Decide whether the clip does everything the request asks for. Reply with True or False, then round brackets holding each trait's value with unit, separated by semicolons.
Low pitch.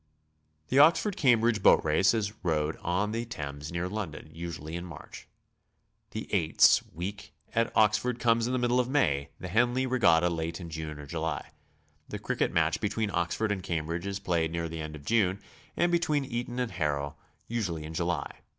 True (90 Hz)